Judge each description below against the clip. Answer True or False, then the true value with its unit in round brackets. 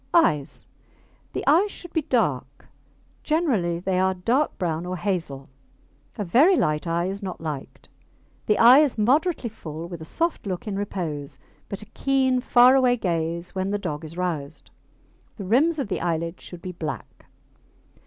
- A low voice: False (190 Hz)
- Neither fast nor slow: True (165 wpm)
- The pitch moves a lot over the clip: True (7.1 semitones)